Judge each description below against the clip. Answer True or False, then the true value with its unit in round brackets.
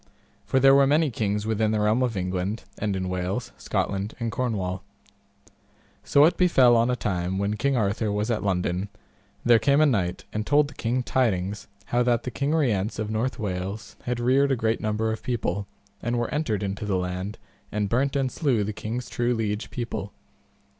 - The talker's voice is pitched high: False (110 Hz)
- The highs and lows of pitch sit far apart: False (3.8 semitones)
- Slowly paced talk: False (195 wpm)